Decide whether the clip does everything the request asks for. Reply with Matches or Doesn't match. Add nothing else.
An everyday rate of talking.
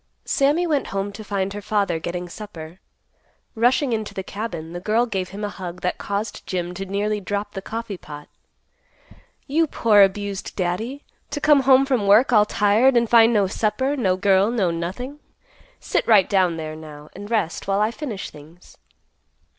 Matches